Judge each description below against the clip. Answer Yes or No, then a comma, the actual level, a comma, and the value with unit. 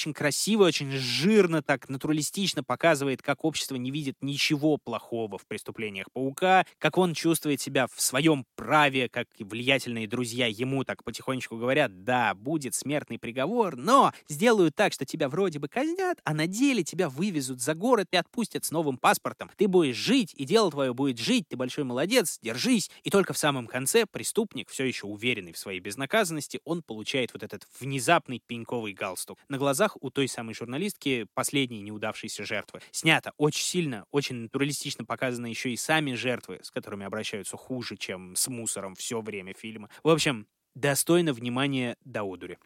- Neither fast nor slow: No, fast, 170 wpm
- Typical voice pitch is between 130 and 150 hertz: Yes, low, 135 Hz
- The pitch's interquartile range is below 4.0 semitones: No, average, 4.8 semitones